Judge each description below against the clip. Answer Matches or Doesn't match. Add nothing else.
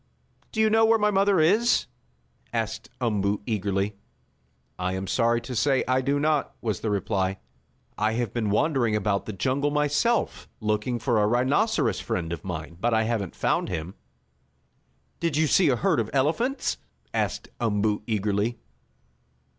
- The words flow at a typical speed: Matches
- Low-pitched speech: Matches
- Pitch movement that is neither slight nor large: Doesn't match